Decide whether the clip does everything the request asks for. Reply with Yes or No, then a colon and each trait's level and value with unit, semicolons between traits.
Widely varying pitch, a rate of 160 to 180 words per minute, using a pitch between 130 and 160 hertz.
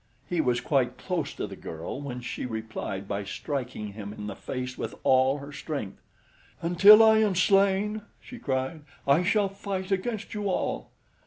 Yes: wide, 8.1 semitones; average, 170 wpm; medium, 140 Hz